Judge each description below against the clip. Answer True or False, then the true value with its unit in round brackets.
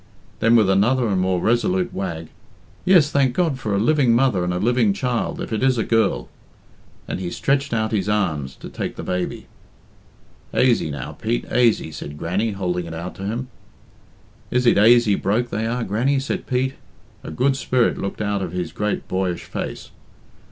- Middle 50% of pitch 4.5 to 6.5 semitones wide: True (5.2 semitones)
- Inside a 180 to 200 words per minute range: True (185 wpm)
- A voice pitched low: True (110 Hz)